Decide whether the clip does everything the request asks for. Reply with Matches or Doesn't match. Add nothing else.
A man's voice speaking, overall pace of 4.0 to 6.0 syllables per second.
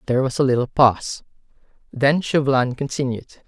Doesn't match